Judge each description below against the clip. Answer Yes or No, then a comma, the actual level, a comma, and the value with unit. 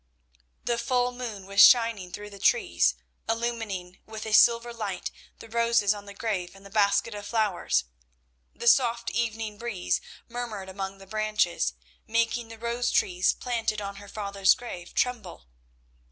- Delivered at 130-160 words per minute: Yes, average, 155 wpm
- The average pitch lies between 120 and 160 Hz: No, high, 215 Hz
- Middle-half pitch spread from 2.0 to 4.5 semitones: Yes, average, 3.0 semitones